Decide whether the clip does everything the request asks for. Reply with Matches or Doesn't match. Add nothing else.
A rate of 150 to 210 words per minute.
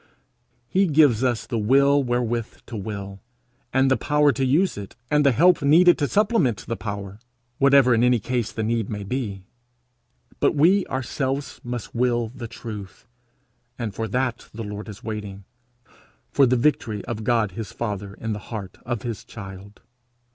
Matches